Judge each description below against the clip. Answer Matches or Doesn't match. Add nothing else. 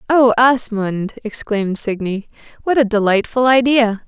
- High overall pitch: Matches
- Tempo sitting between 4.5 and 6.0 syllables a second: Matches